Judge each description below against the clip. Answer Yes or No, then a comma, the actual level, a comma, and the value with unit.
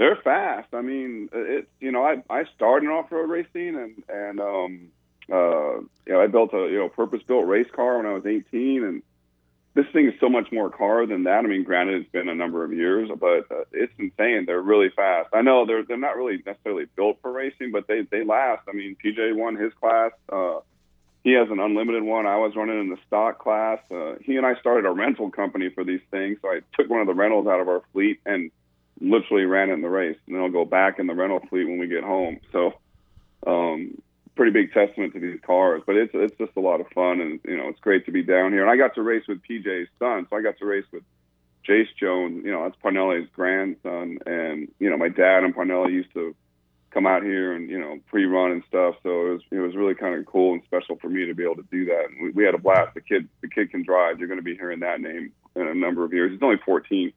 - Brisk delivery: Yes, fast, 255 wpm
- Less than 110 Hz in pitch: Yes, low, 100 Hz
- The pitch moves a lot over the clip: Yes, wide, 6.0 semitones